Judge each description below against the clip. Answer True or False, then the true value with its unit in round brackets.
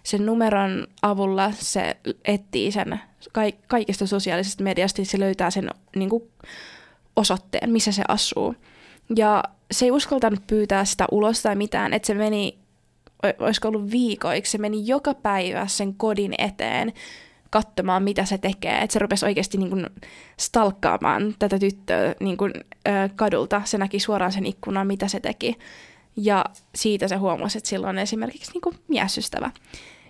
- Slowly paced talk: False (150 wpm)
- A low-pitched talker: False (205 Hz)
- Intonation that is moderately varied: False (1.9 semitones)